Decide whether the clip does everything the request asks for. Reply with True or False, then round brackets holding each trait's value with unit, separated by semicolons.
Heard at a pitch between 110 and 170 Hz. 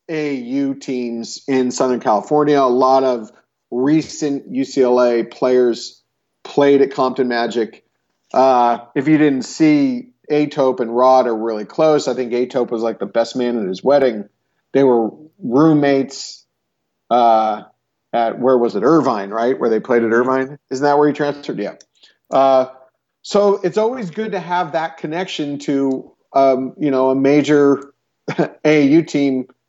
True (135 Hz)